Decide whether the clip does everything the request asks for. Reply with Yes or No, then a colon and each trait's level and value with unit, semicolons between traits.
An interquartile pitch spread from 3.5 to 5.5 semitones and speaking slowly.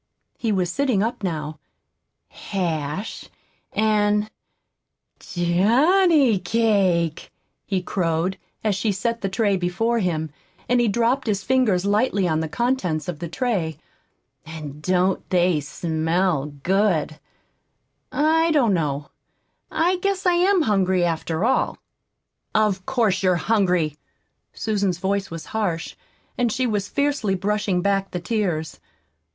Yes: average, 4.7 semitones; slow, 125 wpm